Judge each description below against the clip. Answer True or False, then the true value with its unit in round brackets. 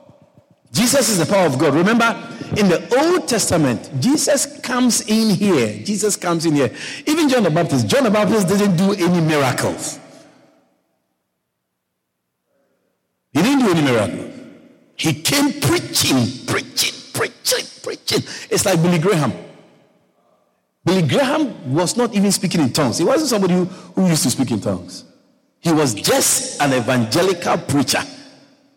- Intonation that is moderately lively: False (9.0 semitones)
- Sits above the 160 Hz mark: True (190 Hz)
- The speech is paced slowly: False (145 wpm)